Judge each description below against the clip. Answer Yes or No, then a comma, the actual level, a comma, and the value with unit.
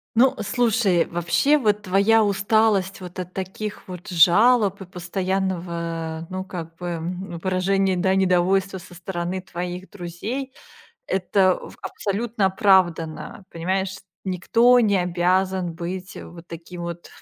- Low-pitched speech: No, medium, 185 Hz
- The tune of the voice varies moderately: No, narrow, 2.2 semitones